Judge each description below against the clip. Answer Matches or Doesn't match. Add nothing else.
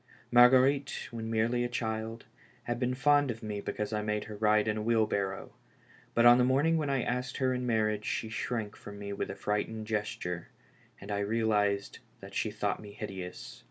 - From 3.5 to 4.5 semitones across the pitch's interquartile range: Doesn't match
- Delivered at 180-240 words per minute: Matches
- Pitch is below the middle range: Matches